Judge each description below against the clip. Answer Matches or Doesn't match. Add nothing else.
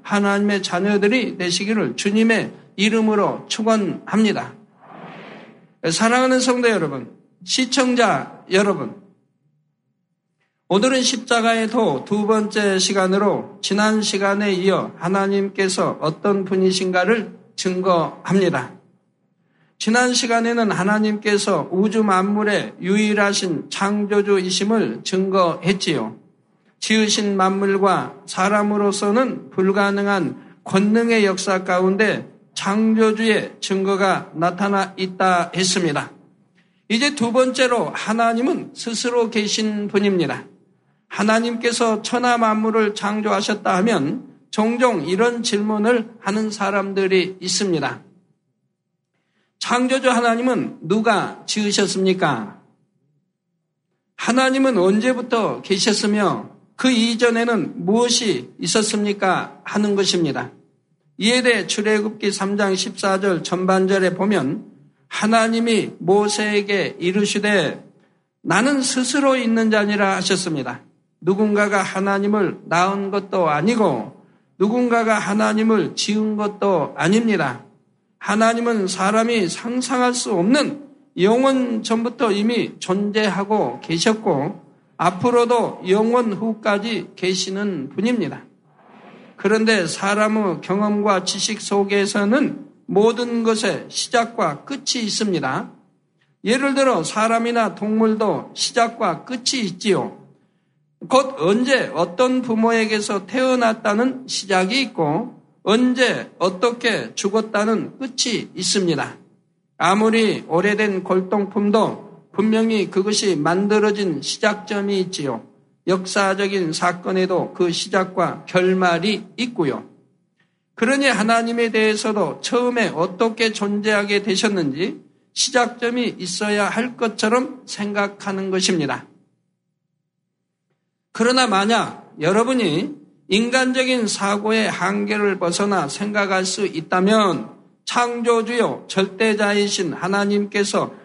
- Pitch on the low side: Doesn't match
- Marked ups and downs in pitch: Doesn't match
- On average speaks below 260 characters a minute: Matches